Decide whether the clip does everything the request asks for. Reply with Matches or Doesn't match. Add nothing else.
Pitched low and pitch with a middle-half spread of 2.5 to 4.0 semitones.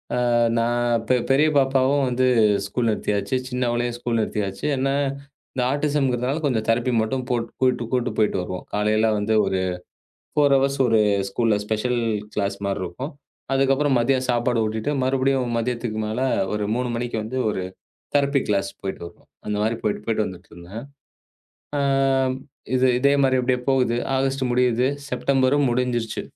Matches